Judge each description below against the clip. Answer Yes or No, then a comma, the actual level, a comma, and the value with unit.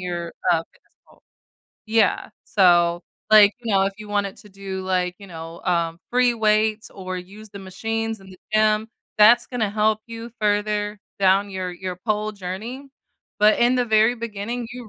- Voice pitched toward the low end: No, high, 210 Hz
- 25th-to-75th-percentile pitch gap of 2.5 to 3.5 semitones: Yes, average, 2.8 semitones